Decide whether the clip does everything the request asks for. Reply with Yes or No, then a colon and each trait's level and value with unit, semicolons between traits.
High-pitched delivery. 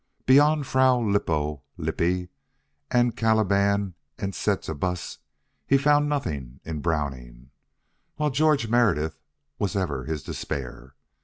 No: low, 100 Hz